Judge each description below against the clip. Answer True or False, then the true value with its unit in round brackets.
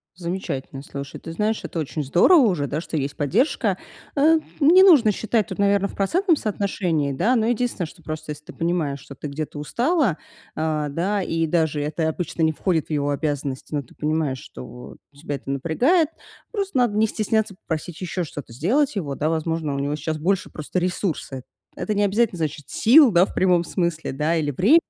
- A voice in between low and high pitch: True (165 Hz)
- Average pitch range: False (5.9 semitones)